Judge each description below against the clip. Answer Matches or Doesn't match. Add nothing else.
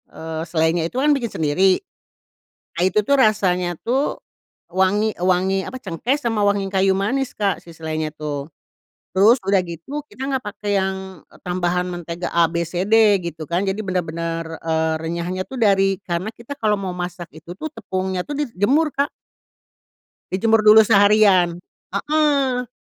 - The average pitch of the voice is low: Doesn't match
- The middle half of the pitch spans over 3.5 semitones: Matches